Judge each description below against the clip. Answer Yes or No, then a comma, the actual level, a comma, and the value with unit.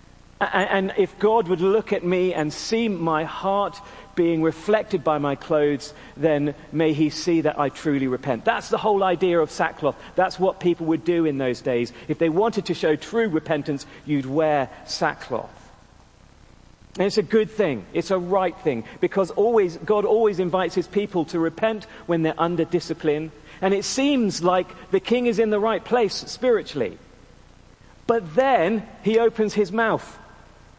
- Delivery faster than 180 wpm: No, average, 170 wpm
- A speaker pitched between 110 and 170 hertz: No, medium, 180 Hz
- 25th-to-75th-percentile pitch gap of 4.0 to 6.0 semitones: Yes, average, 5.0 semitones